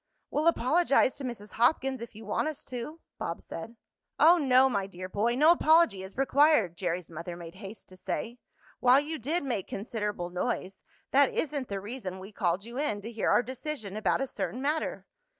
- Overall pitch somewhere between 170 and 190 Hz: No, high, 235 Hz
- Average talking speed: Yes, average, 190 wpm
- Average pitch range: No, wide, 6.2 semitones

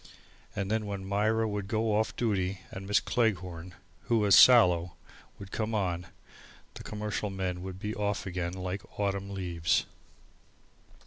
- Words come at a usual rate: Yes, average, 145 wpm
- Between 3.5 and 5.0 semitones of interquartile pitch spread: No, narrow, 2.5 semitones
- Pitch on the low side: Yes, low, 100 Hz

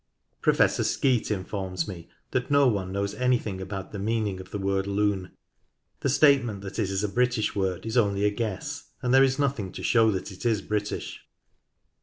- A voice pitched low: Yes, low, 105 Hz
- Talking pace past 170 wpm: Yes, average, 190 wpm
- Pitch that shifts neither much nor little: Yes, average, 4.0 semitones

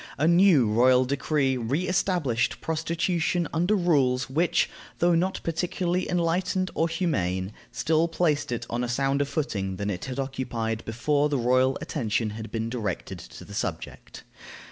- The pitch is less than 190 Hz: Yes, medium, 140 Hz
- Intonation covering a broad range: Yes, wide, 6.0 semitones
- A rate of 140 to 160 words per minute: Yes, average, 150 wpm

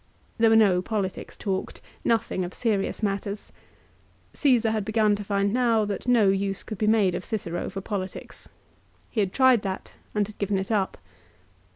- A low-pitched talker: No, high, 205 Hz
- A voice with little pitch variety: Yes, narrow, 2.3 semitones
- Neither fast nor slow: Yes, average, 175 wpm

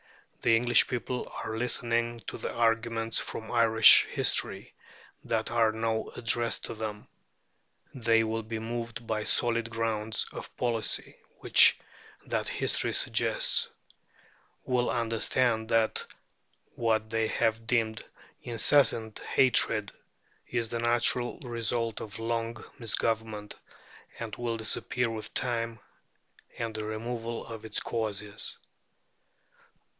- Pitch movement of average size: No, narrow, 1.0 semitones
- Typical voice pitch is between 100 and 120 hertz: Yes, low, 115 Hz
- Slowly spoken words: Yes, slow, 115 wpm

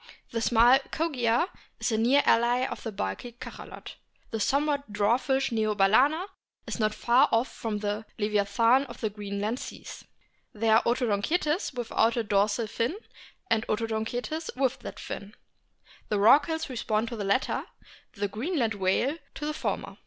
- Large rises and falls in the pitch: No, average, 3.9 semitones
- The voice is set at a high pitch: Yes, high, 230 Hz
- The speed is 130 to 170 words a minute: Yes, average, 155 wpm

